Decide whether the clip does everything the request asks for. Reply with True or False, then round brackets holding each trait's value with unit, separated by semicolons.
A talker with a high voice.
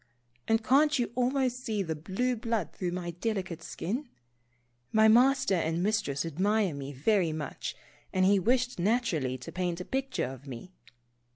True (195 Hz)